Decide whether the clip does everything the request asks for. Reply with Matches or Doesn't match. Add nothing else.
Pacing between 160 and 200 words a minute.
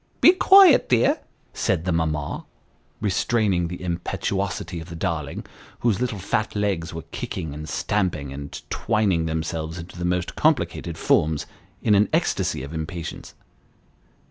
Doesn't match